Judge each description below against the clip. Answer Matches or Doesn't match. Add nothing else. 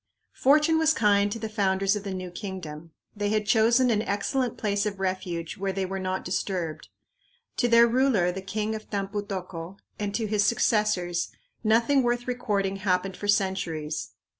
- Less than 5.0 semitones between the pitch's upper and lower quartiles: Matches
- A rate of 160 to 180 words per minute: Matches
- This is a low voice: Doesn't match